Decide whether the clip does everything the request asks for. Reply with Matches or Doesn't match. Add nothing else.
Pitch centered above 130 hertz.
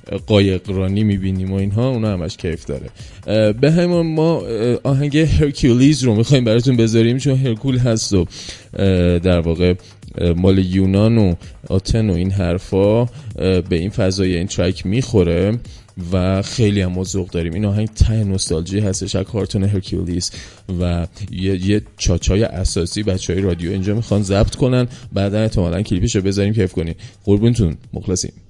Doesn't match